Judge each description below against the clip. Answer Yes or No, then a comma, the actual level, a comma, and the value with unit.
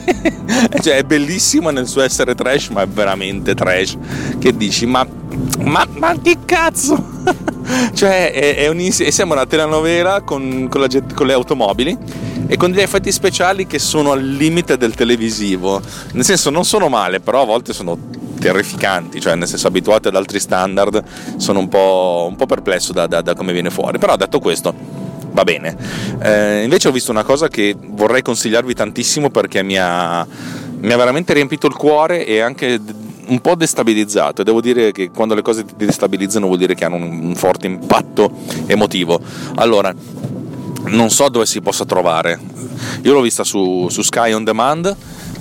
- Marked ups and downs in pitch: Yes, wide, 7.3 semitones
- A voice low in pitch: Yes, low, 120 Hz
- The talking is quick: Yes, fast, 175 wpm